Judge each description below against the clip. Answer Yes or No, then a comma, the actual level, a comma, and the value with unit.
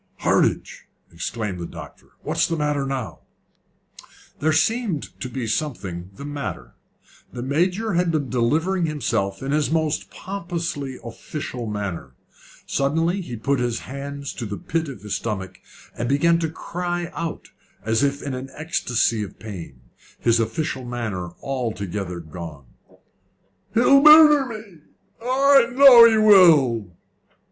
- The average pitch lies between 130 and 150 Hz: Yes, medium, 140 Hz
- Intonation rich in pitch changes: Yes, wide, 7.1 semitones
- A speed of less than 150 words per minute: Yes, slow, 135 wpm